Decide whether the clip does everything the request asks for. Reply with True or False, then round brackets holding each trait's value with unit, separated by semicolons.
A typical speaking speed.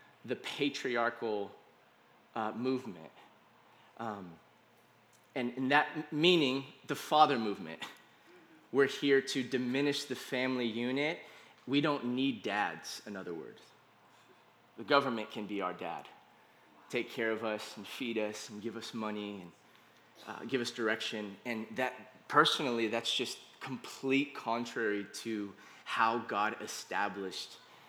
False (125 wpm)